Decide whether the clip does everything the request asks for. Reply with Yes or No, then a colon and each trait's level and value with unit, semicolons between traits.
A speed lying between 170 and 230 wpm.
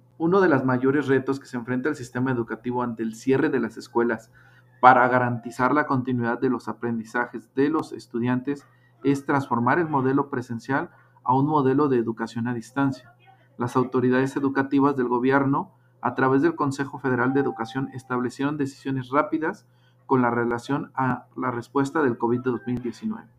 No: average, 160 wpm